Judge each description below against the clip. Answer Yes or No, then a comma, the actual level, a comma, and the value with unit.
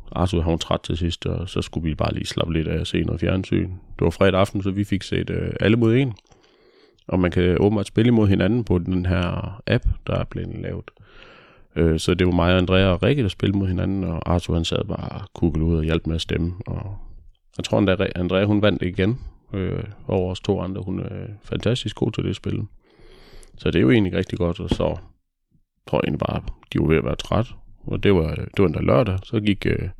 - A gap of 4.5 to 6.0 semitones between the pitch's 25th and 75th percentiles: No, average, 3.2 semitones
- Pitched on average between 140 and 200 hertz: No, very low, 95 Hz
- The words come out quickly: Yes, fast, 245 wpm